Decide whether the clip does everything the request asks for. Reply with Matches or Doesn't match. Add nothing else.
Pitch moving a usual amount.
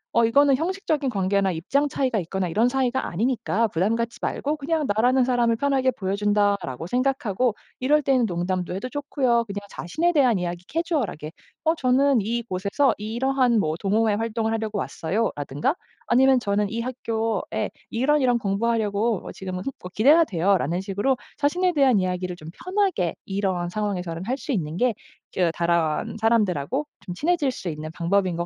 Doesn't match